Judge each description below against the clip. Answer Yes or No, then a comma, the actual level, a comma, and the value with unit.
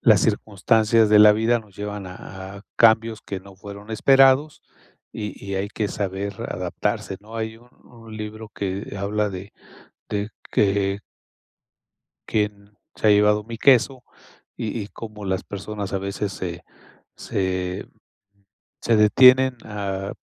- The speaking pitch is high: No, low, 105 Hz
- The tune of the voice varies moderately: No, narrow, 2.1 semitones